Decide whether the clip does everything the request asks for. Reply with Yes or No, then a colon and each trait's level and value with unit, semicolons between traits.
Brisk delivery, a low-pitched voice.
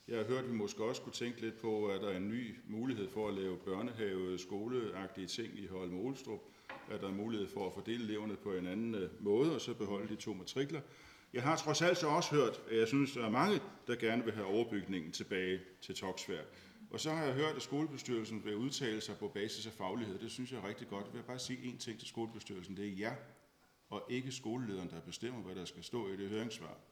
Yes: fast, 245 wpm; low, 110 Hz